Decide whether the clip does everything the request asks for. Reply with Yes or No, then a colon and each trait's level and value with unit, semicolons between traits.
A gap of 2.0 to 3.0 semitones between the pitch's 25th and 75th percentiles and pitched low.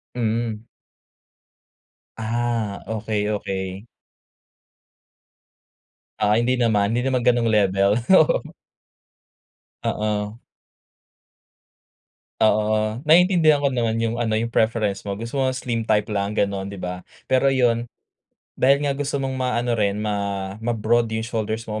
Yes: narrow, 2.6 semitones; low, 115 Hz